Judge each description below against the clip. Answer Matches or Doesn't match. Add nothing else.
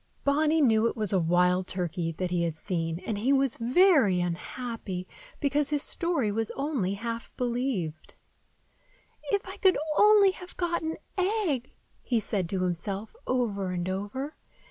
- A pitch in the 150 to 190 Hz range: Doesn't match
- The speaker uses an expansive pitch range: Matches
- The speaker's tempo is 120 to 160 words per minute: Matches